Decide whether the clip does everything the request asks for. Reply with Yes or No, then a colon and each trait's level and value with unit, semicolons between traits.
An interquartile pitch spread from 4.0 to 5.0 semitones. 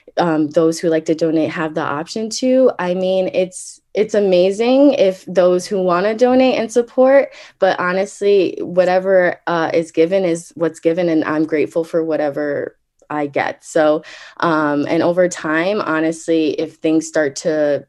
No: average, 3.3 semitones